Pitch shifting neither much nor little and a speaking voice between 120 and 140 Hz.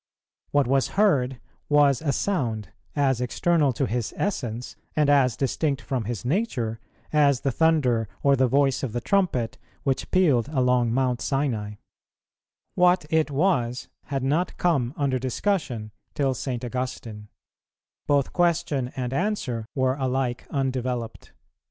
Yes: average, 3.3 semitones; low, 135 Hz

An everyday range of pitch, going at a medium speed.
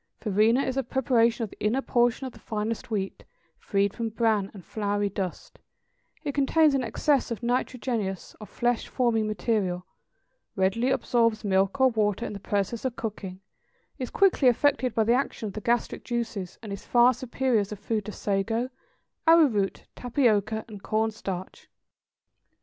Yes: average, 3.3 semitones; average, 165 wpm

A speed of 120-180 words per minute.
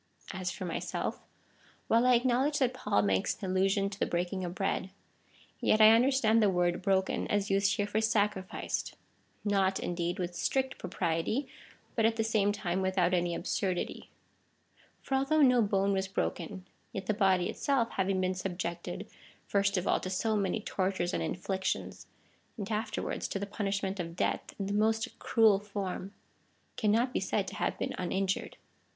Yes: average, 175 wpm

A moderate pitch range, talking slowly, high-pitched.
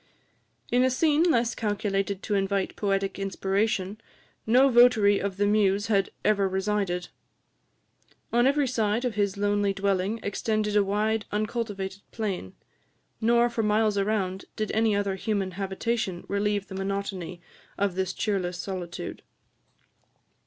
No: narrow, 2.2 semitones; slow, 130 wpm; high, 205 Hz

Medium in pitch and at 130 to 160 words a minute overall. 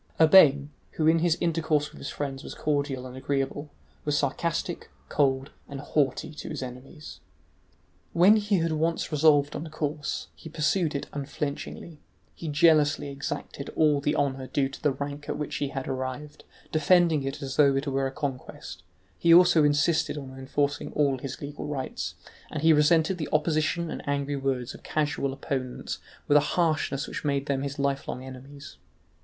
No: medium, 145 Hz; average, 170 wpm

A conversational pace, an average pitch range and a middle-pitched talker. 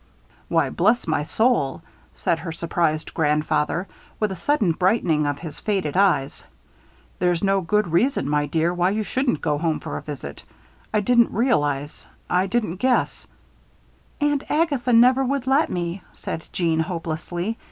No: average, 155 wpm; wide, 6.3 semitones; medium, 180 Hz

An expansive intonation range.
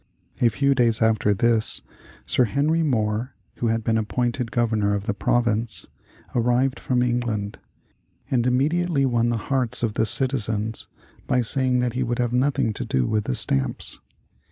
No: narrow, 2.6 semitones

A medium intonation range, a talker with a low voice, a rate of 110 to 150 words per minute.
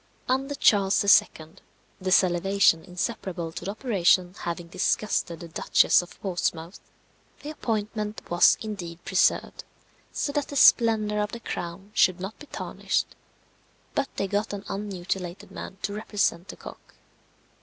No: average, 3.5 semitones; high, 195 Hz; average, 140 wpm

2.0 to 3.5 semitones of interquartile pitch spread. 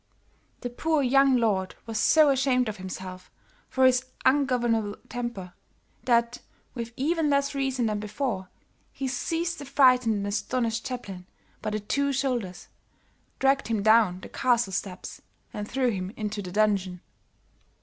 No: average, 4.5 semitones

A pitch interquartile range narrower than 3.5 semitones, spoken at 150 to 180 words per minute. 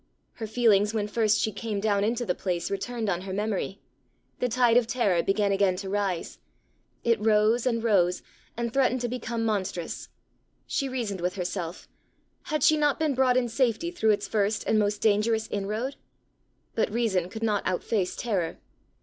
Yes: average, 3.1 semitones; average, 175 wpm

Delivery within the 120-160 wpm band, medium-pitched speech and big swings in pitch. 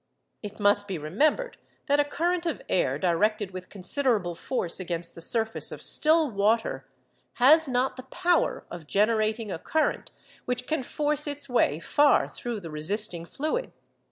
No: average, 155 wpm; high, 225 Hz; wide, 7.8 semitones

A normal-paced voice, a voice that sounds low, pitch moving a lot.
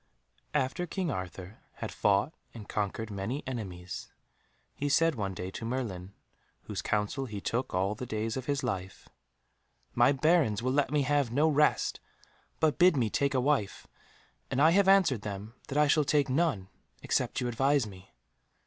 Yes: average, 170 wpm; low, 125 Hz; wide, 5.9 semitones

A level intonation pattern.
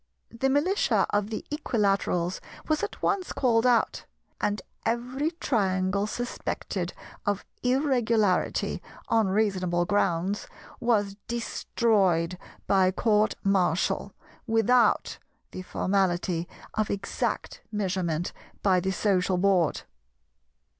No: average, 3.9 semitones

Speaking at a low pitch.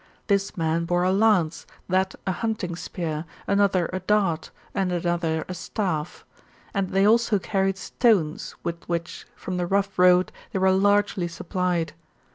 No: medium, 185 Hz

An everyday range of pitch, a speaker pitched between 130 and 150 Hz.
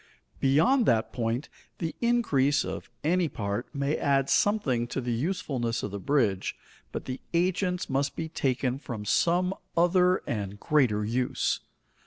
No: wide, 6.6 semitones; medium, 140 Hz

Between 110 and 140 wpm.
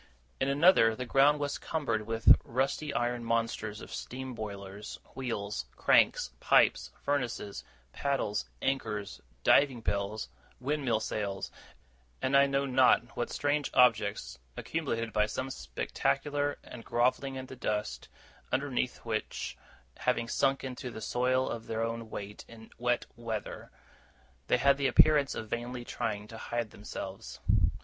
Yes: slow, 135 wpm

